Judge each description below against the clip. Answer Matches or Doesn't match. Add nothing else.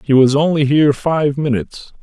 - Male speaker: Matches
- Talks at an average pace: Matches